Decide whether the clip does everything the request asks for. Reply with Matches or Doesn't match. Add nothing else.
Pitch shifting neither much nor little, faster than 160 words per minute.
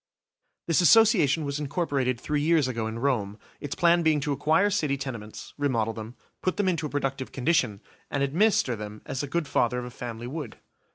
Matches